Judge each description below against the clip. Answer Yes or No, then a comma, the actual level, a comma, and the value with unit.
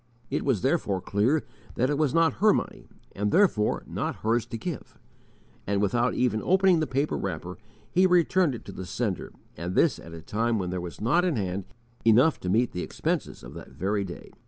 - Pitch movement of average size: No, wide, 8.1 semitones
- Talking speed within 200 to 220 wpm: Yes, fast, 205 wpm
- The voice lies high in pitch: No, low, 115 Hz